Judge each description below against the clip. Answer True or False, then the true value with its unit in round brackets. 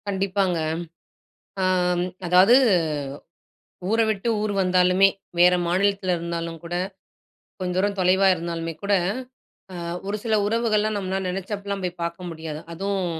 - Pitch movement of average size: False (2.3 semitones)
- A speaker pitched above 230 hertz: False (185 Hz)